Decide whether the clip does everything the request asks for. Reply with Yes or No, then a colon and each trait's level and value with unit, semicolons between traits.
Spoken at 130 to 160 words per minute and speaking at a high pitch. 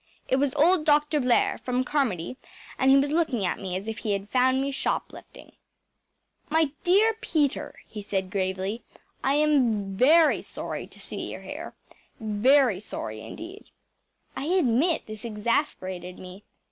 Yes: average, 155 wpm; very high, 255 Hz